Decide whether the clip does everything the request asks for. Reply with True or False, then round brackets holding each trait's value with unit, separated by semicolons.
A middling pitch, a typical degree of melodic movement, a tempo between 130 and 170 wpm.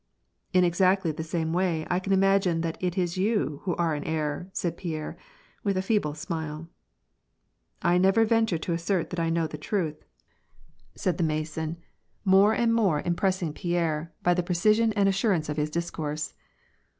False (175 Hz; 3.2 semitones; 190 wpm)